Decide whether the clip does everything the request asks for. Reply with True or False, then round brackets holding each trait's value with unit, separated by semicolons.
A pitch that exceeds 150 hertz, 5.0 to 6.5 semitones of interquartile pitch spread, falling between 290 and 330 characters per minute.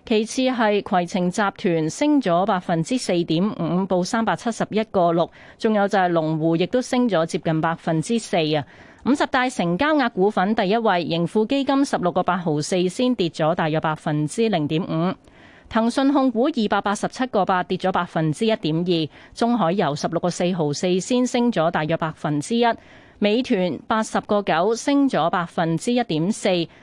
False (185 Hz; 5.5 semitones; 275 characters per minute)